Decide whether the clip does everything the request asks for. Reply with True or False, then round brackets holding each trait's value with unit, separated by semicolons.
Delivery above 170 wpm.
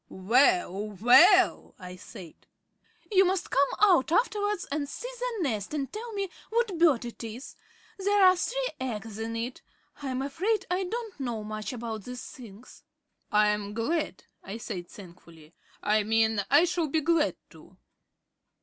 False (155 wpm)